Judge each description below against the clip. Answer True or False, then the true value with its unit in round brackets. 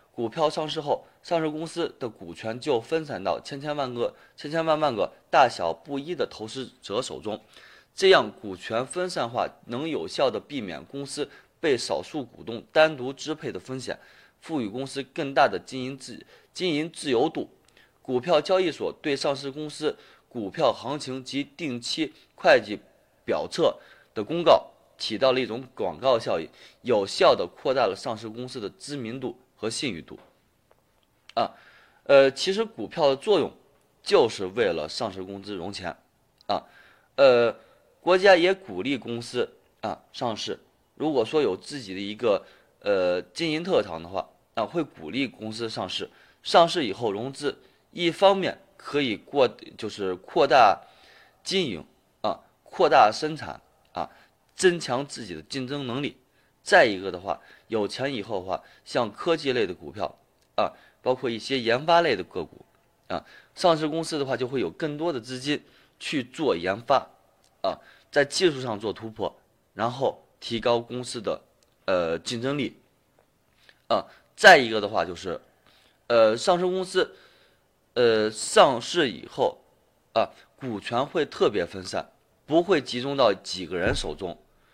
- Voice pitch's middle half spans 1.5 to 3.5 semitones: False (5.5 semitones)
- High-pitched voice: False (140 Hz)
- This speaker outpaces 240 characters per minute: False (225 characters per minute)